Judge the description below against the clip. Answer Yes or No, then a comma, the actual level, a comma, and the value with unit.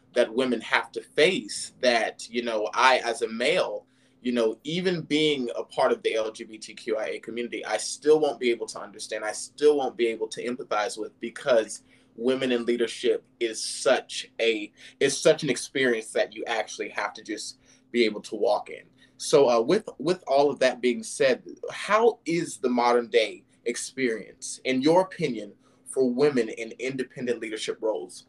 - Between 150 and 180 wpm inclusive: Yes, average, 175 wpm